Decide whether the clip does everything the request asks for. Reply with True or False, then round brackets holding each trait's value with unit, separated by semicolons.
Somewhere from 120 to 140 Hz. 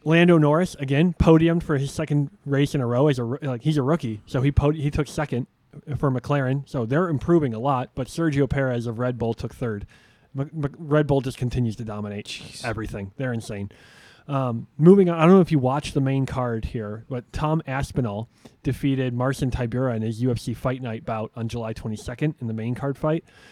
True (135 Hz)